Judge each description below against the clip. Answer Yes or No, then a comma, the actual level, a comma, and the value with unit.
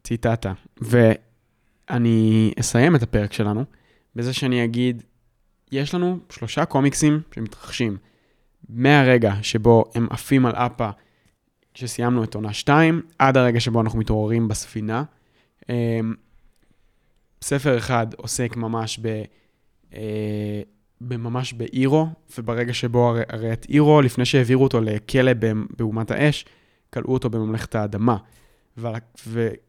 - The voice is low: Yes, low, 115 Hz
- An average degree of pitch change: No, narrow, 2.2 semitones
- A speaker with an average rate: Yes, average, 110 wpm